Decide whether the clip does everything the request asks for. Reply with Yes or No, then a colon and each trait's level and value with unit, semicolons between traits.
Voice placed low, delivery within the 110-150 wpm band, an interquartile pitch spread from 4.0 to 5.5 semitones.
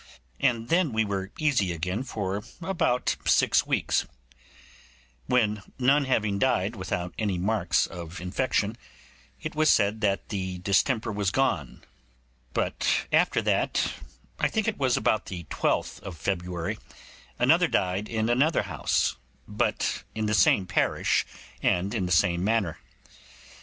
Yes: low, 105 Hz; slow, 135 wpm; average, 4.9 semitones